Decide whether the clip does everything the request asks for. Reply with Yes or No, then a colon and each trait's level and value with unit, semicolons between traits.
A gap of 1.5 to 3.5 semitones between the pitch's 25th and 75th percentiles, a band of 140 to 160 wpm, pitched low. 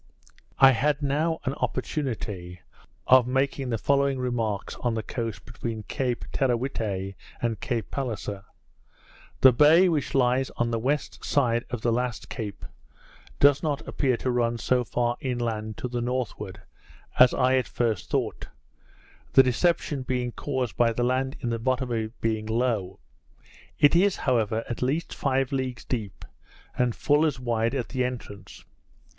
Yes: average, 2.7 semitones; average, 155 wpm; low, 125 Hz